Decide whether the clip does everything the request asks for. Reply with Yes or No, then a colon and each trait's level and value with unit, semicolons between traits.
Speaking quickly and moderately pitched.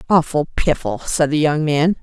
No: average, 180 wpm; medium, 155 Hz